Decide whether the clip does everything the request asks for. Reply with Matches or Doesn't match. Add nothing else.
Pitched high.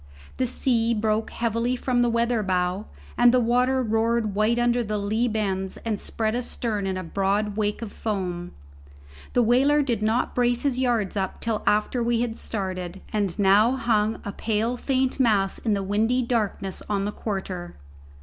Matches